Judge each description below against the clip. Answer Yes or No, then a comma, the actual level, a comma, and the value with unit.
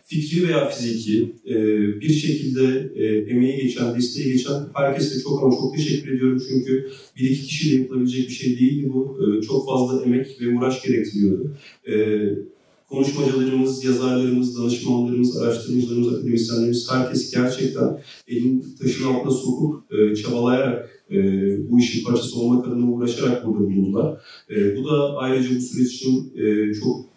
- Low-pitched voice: Yes, low, 125 Hz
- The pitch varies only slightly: Yes, narrow, 1.7 semitones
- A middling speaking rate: Yes, average, 125 wpm